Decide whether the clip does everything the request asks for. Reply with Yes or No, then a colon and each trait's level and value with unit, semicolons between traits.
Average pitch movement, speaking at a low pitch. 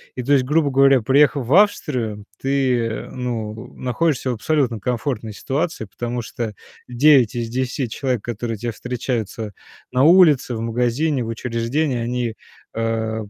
Yes: average, 3.2 semitones; low, 125 Hz